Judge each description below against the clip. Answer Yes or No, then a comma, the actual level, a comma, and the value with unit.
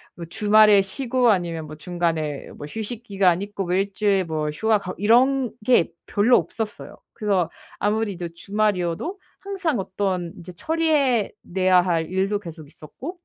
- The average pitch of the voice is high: Yes, high, 195 Hz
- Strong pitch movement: No, average, 4.4 semitones